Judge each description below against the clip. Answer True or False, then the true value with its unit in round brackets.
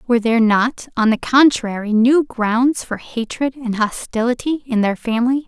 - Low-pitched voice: False (240 Hz)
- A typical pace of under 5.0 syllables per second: True (4.8 syllables/s)